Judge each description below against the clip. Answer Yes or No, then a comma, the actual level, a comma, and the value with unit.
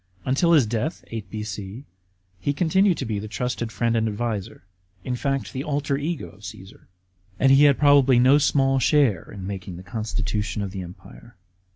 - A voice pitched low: Yes, low, 120 Hz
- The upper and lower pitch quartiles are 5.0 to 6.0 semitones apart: Yes, average, 5.3 semitones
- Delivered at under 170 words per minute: No, average, 180 wpm